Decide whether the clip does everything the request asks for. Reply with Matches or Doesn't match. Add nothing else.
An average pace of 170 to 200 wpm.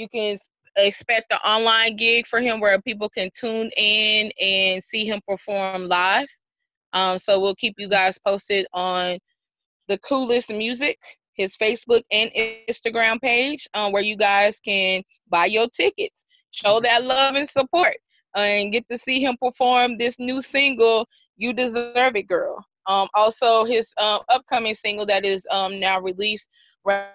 Doesn't match